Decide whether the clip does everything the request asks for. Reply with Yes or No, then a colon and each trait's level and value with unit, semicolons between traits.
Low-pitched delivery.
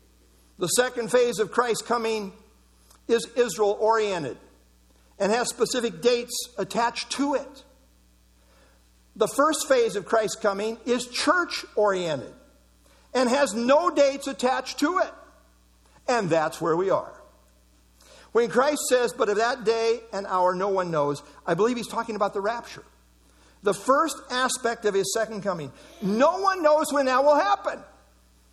No: high, 225 Hz